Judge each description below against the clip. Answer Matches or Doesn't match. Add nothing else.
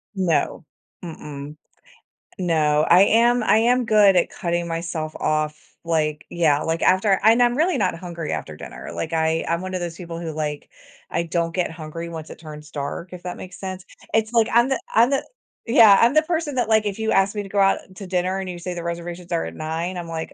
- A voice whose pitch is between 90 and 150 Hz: Doesn't match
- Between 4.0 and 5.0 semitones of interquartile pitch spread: Matches